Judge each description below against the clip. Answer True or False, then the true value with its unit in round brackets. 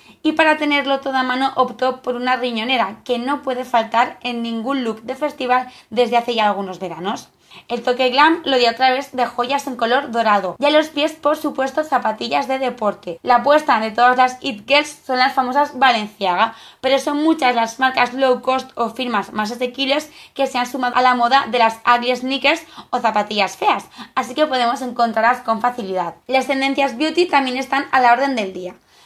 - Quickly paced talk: True (200 wpm)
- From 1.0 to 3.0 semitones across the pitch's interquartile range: True (2.6 semitones)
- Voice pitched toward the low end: False (255 Hz)